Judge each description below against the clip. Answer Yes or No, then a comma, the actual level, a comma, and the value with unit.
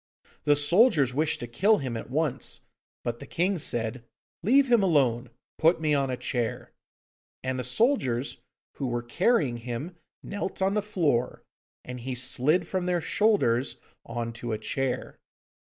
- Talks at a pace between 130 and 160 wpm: Yes, average, 155 wpm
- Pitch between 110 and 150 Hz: Yes, medium, 140 Hz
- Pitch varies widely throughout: Yes, wide, 7.0 semitones